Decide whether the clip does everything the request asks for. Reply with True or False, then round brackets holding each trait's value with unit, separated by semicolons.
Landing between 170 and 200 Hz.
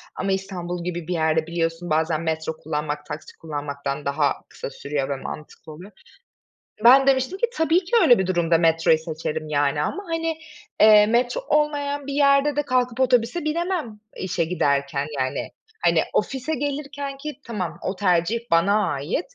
True (185 Hz)